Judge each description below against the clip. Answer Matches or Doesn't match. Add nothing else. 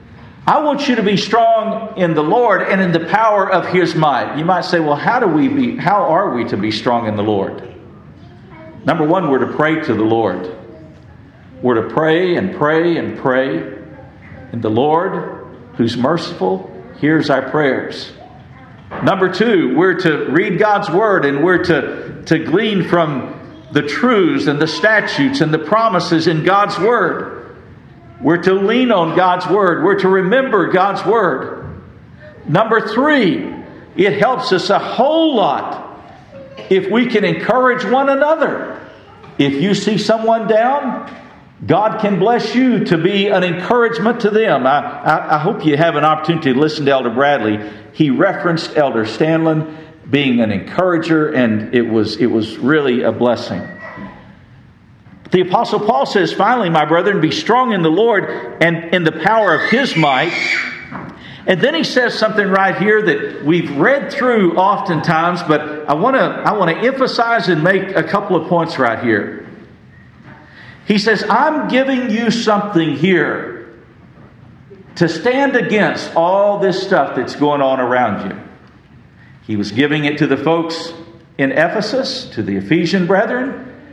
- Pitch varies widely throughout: Matches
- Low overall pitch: Doesn't match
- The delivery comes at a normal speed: Matches